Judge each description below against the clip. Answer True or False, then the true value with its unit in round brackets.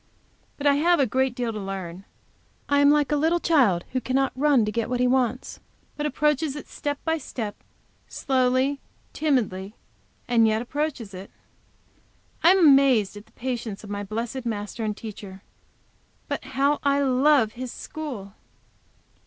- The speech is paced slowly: False (160 wpm)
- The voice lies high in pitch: True (255 Hz)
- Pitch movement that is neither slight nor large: True (4.9 semitones)